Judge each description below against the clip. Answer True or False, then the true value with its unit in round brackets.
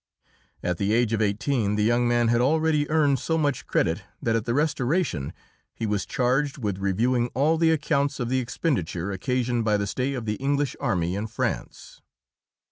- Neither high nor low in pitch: False (120 Hz)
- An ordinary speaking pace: True (185 wpm)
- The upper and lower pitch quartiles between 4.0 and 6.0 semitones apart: True (5.1 semitones)